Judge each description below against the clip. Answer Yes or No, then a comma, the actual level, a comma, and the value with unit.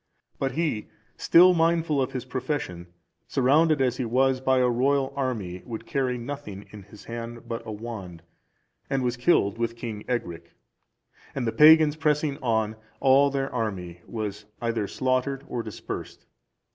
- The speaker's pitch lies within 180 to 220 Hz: No, low, 125 Hz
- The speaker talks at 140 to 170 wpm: Yes, average, 155 wpm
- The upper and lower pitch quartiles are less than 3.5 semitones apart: No, average, 3.8 semitones